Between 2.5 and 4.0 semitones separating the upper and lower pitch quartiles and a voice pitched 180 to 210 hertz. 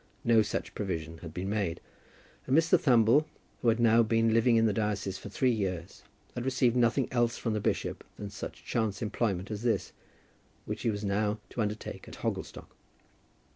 No: average, 2.9 semitones; low, 110 Hz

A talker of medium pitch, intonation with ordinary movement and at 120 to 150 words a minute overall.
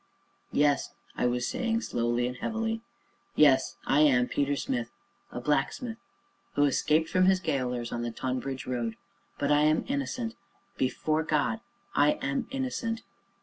No: medium, 145 Hz; wide, 6.9 semitones; average, 145 wpm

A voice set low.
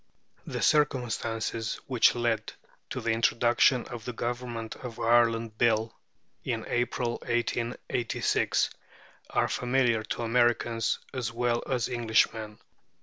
Yes: low, 120 Hz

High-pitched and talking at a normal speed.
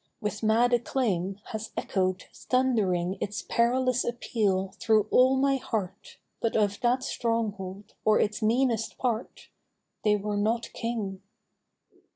No: high, 220 Hz; slow, 125 wpm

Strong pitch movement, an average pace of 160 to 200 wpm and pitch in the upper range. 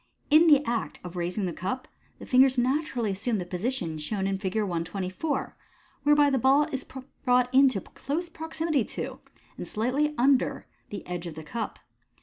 Yes: wide, 6.5 semitones; average, 165 wpm; high, 245 Hz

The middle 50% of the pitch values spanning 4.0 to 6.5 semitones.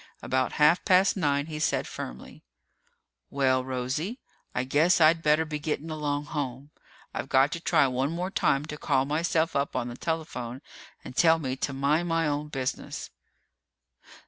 No: average, 3.5 semitones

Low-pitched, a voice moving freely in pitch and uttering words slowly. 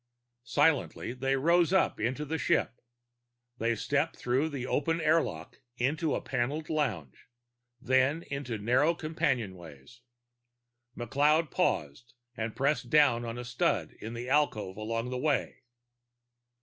No: low, 130 Hz; average, 4.5 semitones; slow, 125 wpm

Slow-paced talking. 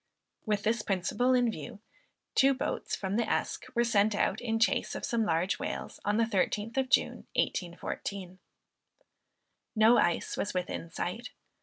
No: average, 155 wpm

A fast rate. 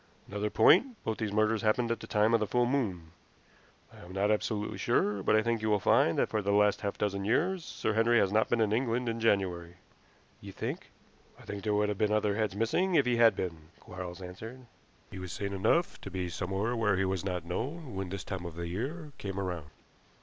Yes: fast, 230 wpm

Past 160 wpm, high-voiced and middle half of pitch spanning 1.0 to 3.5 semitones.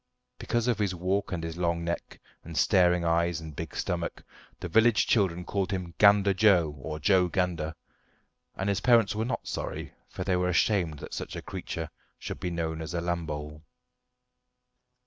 No: average, 175 wpm; very low, 90 Hz; average, 3.1 semitones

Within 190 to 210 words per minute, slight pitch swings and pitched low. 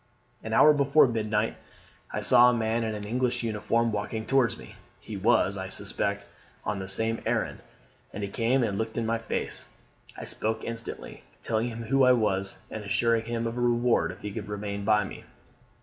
Yes: average, 195 wpm; narrow, 2.2 semitones; low, 110 Hz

